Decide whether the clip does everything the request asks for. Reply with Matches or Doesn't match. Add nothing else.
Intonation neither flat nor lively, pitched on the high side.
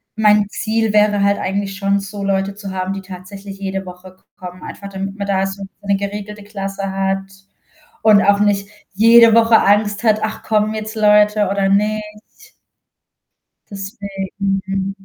Doesn't match